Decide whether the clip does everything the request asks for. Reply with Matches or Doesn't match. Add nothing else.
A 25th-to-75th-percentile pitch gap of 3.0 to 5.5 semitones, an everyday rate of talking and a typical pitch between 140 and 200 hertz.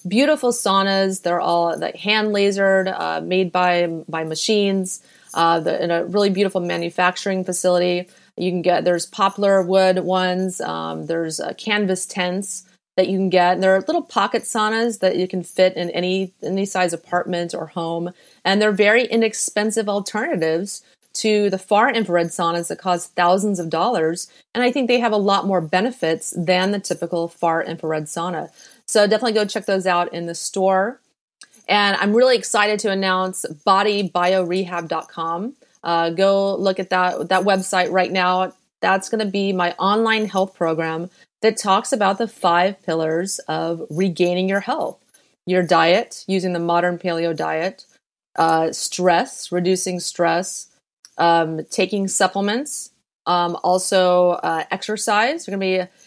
Doesn't match